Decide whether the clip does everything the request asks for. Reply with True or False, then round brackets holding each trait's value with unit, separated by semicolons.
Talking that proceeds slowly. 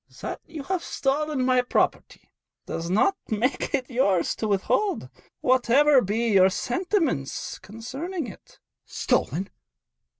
True (125 wpm)